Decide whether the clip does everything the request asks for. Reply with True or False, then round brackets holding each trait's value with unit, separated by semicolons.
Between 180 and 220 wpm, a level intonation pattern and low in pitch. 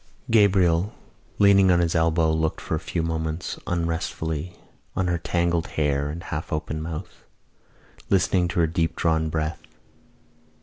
False (140 wpm; 1.8 semitones; 80 Hz)